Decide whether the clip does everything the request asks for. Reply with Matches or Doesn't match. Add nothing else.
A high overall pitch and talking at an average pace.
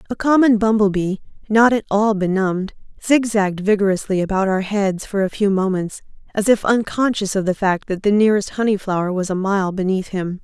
Matches